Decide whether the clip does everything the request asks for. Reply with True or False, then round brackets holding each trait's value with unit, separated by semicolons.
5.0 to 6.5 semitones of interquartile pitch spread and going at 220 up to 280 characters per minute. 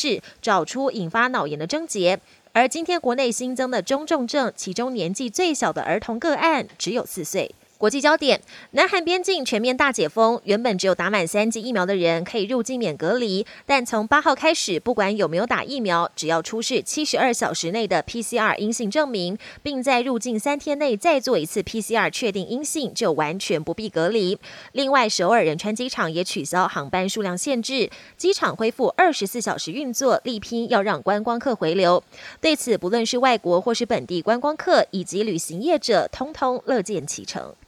False (5.4 semitones; 300 characters per minute)